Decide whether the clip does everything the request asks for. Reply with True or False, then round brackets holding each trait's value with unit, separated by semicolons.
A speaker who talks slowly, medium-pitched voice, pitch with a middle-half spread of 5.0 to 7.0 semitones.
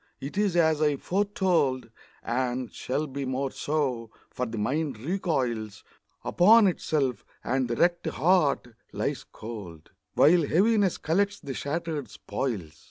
True (130 wpm; 145 Hz; 5.5 semitones)